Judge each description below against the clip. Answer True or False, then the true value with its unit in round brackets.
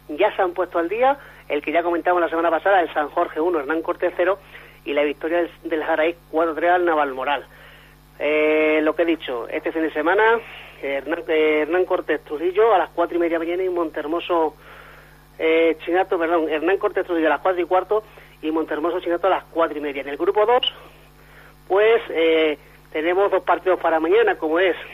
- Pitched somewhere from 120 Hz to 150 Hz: False (170 Hz)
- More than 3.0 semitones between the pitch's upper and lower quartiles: False (2.7 semitones)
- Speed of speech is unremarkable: False (200 wpm)